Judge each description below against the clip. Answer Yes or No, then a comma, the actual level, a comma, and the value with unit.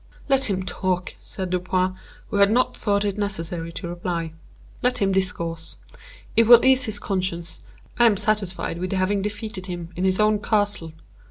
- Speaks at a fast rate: No, average, 170 wpm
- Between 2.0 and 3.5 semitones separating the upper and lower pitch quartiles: Yes, average, 2.8 semitones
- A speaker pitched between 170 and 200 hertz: Yes, high, 190 Hz